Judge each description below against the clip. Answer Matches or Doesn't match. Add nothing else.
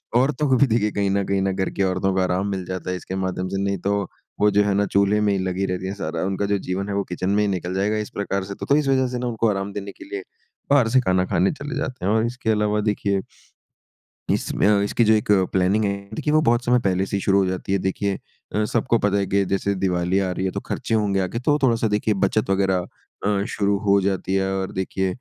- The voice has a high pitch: Doesn't match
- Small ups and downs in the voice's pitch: Matches